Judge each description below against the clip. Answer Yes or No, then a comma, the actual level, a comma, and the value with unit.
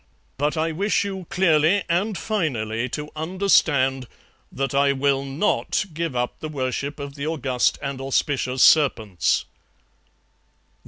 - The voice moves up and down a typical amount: Yes, average, 3.8 semitones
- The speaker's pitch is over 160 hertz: No, medium, 145 Hz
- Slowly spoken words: Yes, slow, 125 wpm